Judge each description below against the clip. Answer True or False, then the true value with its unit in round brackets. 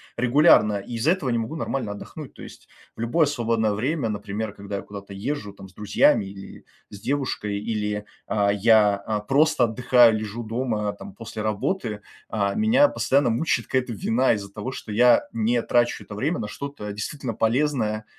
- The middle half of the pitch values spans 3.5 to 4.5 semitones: True (3.8 semitones)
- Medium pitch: False (110 Hz)